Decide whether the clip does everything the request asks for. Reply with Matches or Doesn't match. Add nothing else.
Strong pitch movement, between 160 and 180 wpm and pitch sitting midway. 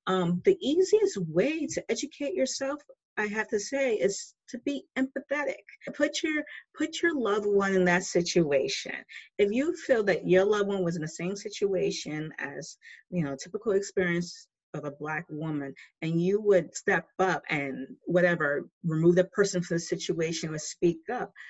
Doesn't match